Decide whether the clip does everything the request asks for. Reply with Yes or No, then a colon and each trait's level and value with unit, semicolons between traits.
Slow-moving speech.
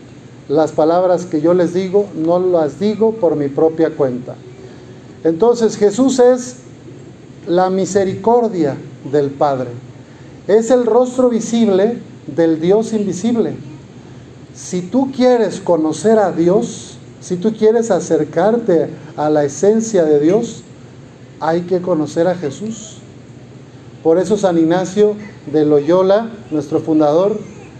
Yes: slow, 120 wpm